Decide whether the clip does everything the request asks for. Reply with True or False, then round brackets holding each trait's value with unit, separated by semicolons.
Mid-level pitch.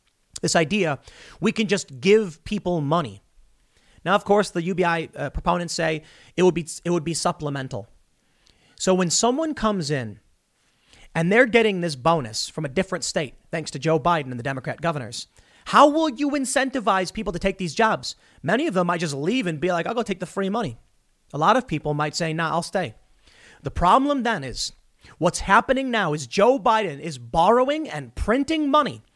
True (175 Hz)